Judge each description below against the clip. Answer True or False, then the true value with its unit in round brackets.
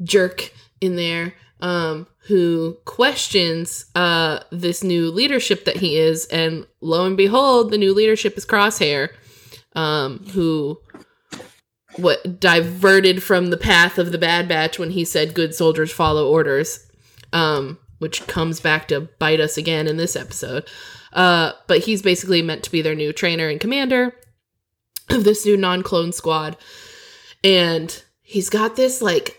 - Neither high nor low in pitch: True (170 Hz)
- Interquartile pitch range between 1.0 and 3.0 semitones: False (3.6 semitones)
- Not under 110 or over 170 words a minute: True (150 wpm)